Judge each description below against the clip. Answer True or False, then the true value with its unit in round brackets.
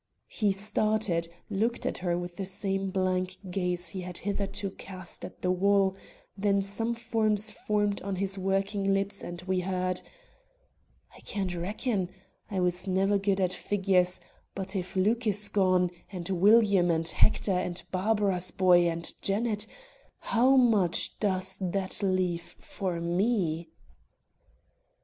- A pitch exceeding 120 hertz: True (190 Hz)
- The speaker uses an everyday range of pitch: False (2.0 semitones)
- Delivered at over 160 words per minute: False (140 wpm)